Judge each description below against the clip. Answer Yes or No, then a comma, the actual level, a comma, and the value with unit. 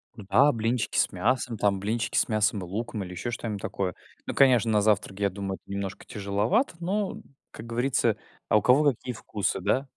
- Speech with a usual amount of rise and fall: Yes, average, 3.8 semitones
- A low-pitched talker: Yes, low, 110 Hz